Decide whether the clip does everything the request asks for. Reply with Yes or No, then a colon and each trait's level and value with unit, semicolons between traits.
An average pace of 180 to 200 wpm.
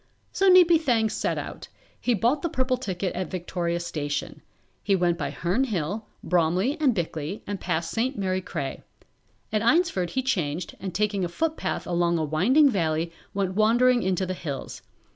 No: average, 170 wpm